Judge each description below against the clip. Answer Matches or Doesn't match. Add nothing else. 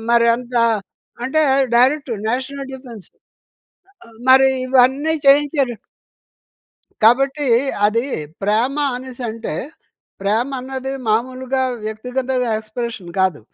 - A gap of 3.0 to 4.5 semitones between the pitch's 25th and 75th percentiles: Doesn't match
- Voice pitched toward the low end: Doesn't match